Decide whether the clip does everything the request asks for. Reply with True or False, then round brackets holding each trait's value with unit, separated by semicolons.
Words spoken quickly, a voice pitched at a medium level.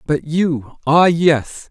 False (105 wpm; 155 Hz)